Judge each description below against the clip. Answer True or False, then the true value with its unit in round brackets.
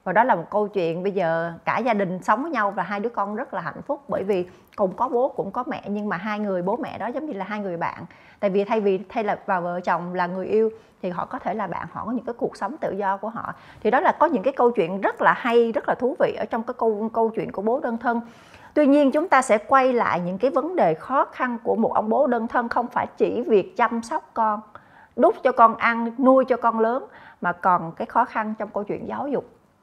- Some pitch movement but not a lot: True (3.7 semitones)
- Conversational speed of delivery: False (280 wpm)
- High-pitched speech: True (225 Hz)